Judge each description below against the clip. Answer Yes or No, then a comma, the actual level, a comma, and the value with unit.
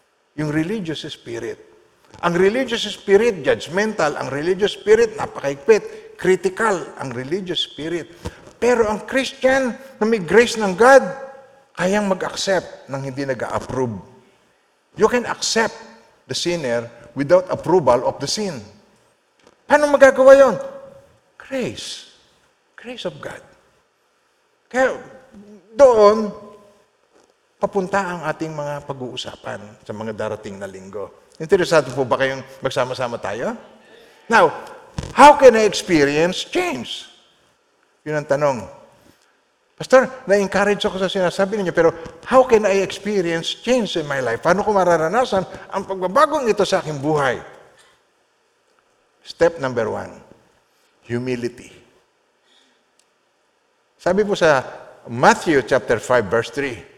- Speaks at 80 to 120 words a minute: Yes, average, 115 wpm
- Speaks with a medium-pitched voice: No, high, 205 Hz